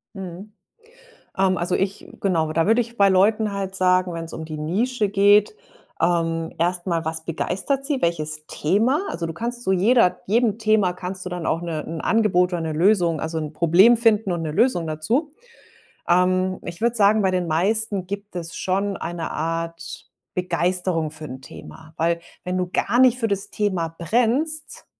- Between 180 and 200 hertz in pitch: Yes, medium, 185 Hz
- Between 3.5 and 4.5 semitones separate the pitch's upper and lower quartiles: Yes, average, 4.1 semitones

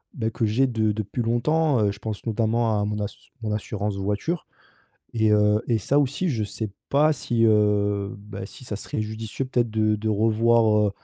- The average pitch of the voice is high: No, low, 110 Hz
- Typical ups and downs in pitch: No, narrow, 2.1 semitones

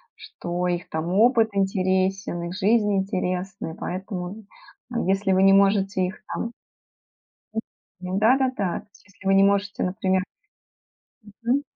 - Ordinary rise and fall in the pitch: No, narrow, 2.0 semitones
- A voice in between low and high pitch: No, high, 195 Hz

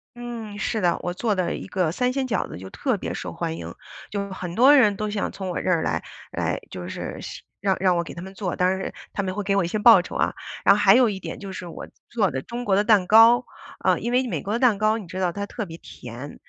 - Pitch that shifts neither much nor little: Yes, average, 3.7 semitones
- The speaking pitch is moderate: No, high, 195 Hz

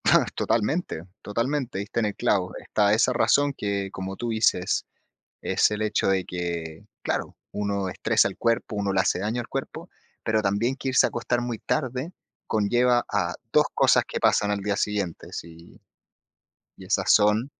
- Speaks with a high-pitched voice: No, low, 105 Hz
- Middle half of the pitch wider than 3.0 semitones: Yes, average, 3.6 semitones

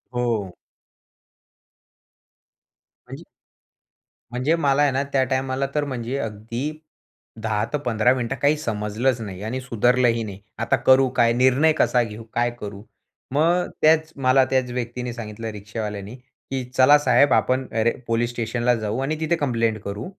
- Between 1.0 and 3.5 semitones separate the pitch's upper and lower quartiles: Yes, average, 3.1 semitones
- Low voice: Yes, low, 125 Hz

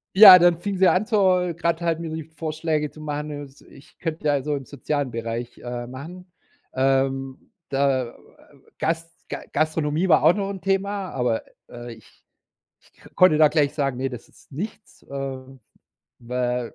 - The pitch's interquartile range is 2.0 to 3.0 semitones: No, average, 4.3 semitones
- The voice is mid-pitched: Yes, medium, 150 Hz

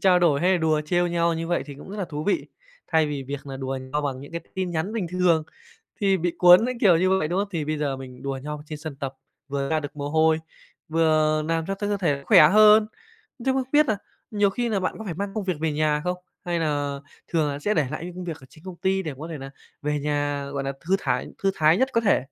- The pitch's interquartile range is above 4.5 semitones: No, average, 4.2 semitones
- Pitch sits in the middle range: Yes, medium, 160 Hz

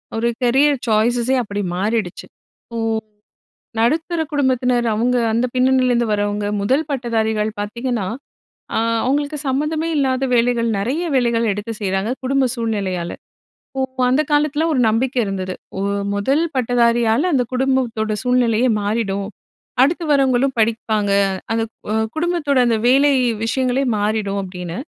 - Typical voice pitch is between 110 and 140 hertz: No, high, 240 Hz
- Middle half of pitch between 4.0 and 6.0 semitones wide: No, average, 3.6 semitones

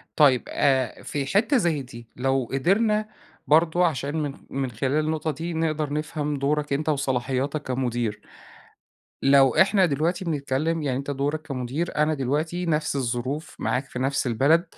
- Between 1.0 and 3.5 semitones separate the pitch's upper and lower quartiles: Yes, average, 3.1 semitones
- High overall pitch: No, medium, 145 Hz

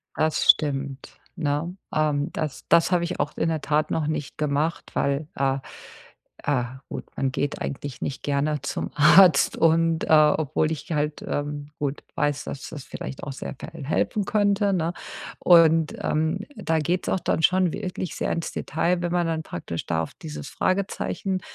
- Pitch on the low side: No, medium, 155 Hz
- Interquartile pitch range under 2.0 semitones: No, average, 2.8 semitones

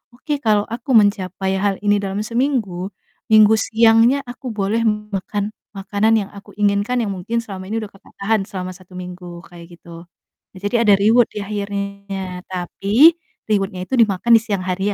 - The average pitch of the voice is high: Yes, high, 200 Hz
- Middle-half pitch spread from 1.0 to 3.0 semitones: Yes, average, 2.7 semitones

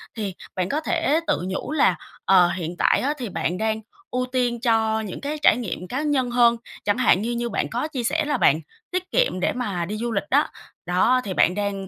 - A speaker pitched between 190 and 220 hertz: No, high, 230 Hz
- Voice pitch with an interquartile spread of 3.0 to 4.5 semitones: No, average, 4.9 semitones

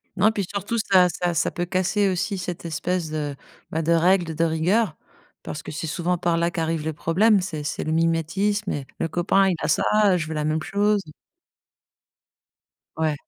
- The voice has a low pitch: No, medium, 170 Hz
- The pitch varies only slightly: No, average, 3.3 semitones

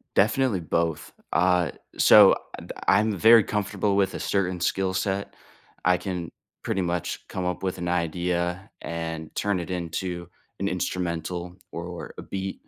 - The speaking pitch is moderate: No, very low, 90 Hz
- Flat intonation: Yes, narrow, 1.9 semitones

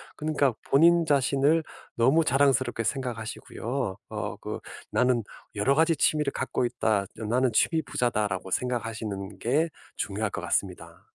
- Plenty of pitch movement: No, average, 4.6 semitones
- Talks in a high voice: No, low, 125 Hz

